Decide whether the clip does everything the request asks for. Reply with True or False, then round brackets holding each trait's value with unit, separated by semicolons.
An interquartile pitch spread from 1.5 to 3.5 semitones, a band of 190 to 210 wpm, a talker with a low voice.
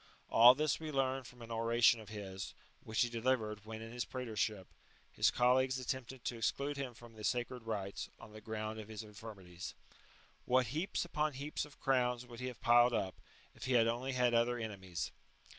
True (2.8 semitones; 195 wpm; 120 Hz)